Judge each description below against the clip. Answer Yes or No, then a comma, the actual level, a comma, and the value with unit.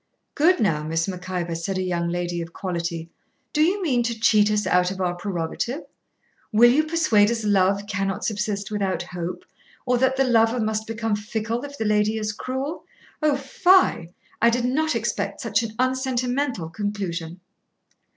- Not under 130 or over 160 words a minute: No, average, 170 wpm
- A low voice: No, high, 210 Hz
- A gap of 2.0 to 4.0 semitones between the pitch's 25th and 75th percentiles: No, average, 5.2 semitones